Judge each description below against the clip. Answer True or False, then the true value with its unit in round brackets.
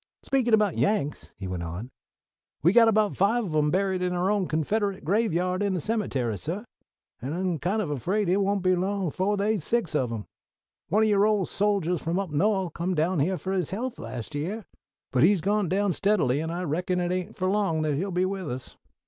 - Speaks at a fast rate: True (215 wpm)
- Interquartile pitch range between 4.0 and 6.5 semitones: True (4.3 semitones)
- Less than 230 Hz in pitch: True (185 Hz)